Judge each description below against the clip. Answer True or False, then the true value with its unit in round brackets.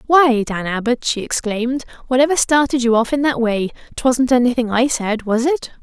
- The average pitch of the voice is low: False (245 Hz)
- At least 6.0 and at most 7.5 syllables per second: False (5.2 syllables/s)